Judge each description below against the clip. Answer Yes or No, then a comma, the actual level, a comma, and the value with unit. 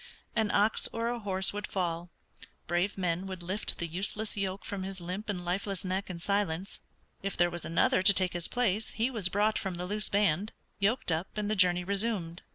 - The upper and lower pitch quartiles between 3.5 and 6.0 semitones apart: No, average, 2.7 semitones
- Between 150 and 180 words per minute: No, fast, 205 wpm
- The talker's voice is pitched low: No, high, 195 Hz